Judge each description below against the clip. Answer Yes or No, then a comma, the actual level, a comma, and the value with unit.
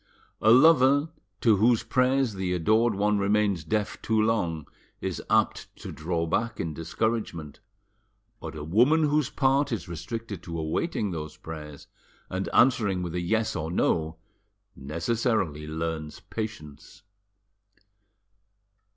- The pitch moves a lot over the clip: Yes, wide, 6.1 semitones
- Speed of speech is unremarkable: No, slow, 125 wpm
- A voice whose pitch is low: Yes, low, 100 Hz